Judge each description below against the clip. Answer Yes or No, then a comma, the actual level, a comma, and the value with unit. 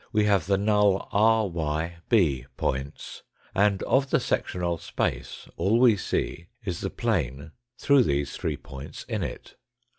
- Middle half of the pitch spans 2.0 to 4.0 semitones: No, wide, 5.5 semitones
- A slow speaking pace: No, average, 155 wpm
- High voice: No, very low, 95 Hz